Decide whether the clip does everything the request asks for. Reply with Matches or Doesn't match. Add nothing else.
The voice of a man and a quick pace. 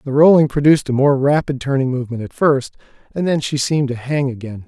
Matches